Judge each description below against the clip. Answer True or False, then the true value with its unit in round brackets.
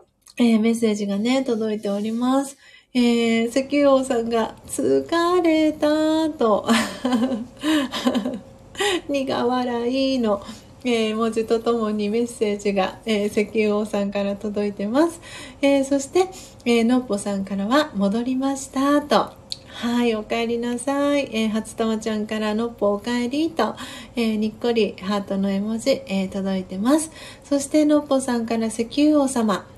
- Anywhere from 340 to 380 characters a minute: False (280 characters per minute)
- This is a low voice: False (235 Hz)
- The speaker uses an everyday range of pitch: True (4.2 semitones)